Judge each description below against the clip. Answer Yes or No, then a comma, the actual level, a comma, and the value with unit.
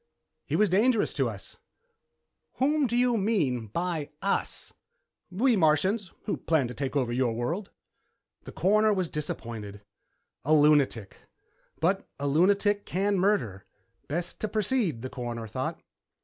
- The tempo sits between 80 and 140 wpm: Yes, slow, 135 wpm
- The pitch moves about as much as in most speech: No, wide, 7.9 semitones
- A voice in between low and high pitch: Yes, medium, 170 Hz